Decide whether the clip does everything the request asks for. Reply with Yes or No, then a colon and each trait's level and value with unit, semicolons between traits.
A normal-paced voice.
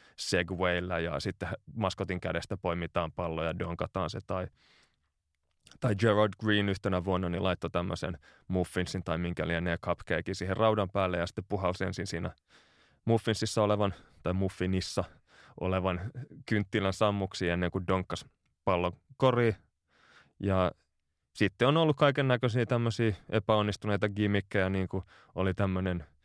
Yes: average, 130 wpm